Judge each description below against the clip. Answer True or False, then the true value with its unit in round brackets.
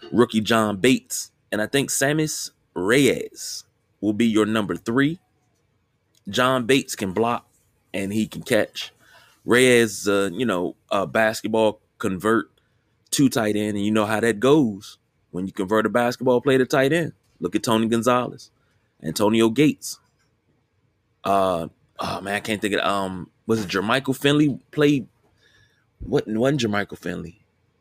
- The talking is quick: False (150 wpm)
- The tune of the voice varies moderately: True (3.4 semitones)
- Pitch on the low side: True (110 Hz)